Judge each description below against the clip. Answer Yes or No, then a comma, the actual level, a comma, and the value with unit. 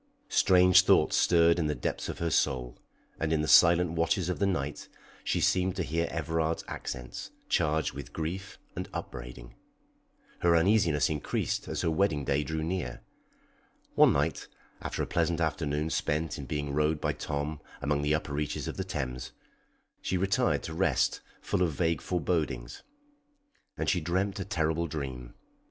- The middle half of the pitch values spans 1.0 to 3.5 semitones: Yes, average, 3.0 semitones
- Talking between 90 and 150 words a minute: No, average, 165 wpm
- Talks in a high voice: No, very low, 80 Hz